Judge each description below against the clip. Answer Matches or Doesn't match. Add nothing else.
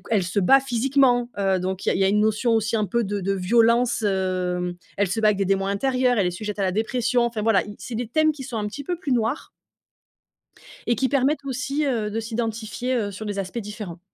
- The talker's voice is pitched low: Doesn't match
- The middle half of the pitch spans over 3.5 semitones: Matches